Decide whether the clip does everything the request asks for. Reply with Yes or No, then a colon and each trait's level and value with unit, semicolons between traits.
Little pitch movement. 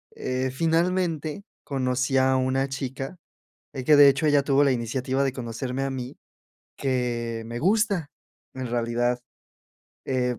Yes: narrow, 2.3 semitones